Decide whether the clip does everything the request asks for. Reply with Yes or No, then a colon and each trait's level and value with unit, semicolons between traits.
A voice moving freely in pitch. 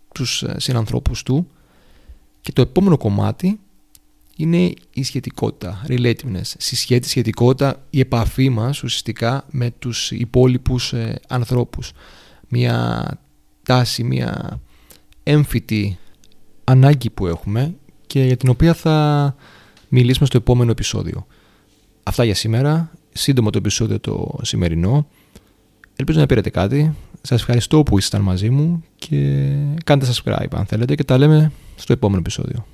No: average, 4.9 semitones